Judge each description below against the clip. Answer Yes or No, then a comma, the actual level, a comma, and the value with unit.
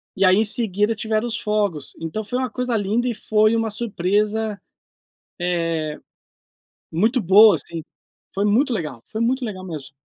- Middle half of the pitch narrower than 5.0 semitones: Yes, average, 3.8 semitones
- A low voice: No, high, 210 Hz